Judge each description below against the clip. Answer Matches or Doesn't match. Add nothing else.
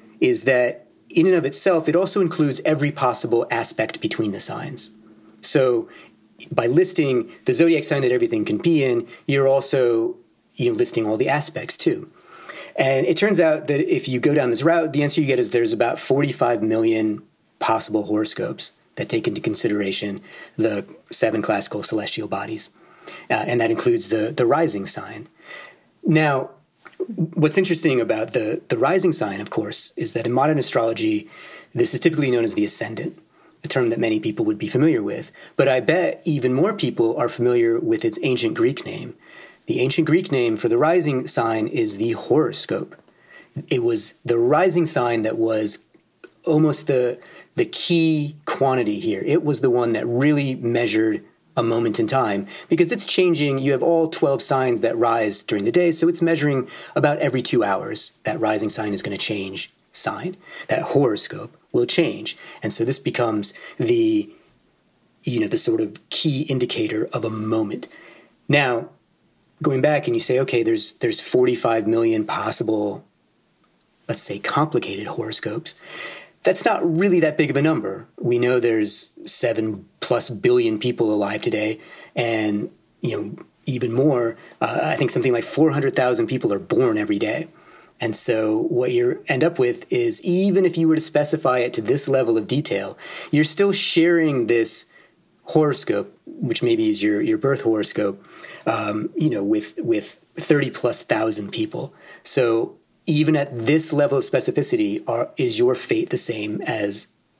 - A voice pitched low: Doesn't match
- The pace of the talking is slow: Doesn't match